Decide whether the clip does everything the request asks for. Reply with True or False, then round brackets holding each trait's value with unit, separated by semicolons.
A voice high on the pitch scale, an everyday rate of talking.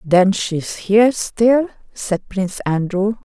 True (200 Hz; 145 wpm)